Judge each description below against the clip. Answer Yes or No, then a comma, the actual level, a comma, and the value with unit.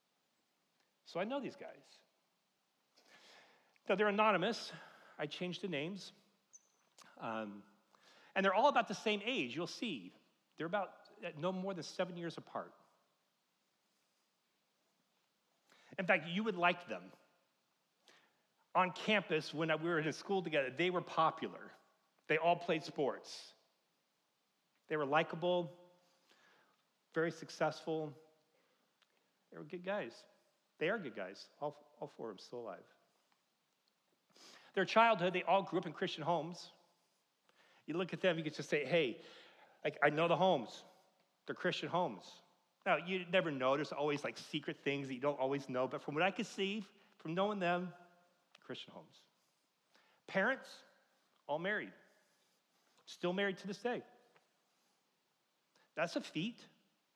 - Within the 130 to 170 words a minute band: Yes, average, 140 wpm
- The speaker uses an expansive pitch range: No, average, 3.8 semitones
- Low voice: No, medium, 175 Hz